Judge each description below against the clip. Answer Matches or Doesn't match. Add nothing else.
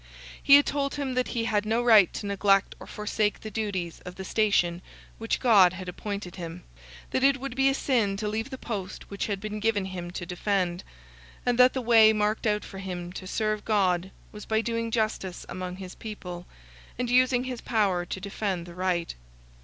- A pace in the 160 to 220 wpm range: Matches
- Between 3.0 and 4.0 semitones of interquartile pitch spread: Matches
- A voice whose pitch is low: Doesn't match